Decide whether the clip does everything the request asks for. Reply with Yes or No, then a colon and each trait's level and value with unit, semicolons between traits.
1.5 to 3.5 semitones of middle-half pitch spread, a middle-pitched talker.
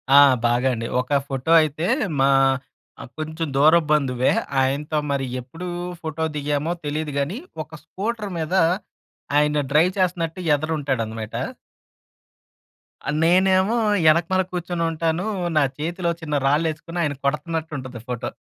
Yes: average, 3.1 semitones; medium, 155 Hz